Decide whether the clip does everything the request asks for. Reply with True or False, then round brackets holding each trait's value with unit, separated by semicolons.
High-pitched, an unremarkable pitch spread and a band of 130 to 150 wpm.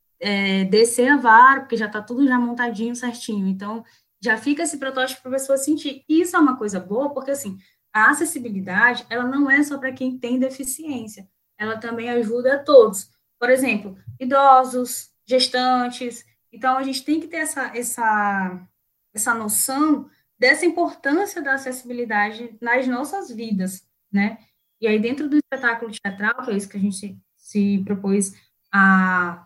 False (245 Hz; 4.1 semitones; 160 wpm)